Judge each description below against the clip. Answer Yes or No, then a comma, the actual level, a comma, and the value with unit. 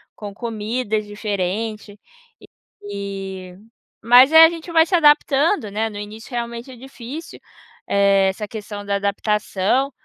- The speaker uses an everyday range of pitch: Yes, average, 4.1 semitones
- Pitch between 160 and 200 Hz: No, high, 215 Hz